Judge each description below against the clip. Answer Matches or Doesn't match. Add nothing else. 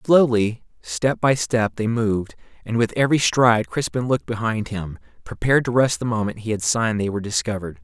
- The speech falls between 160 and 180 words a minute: Doesn't match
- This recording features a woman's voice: Doesn't match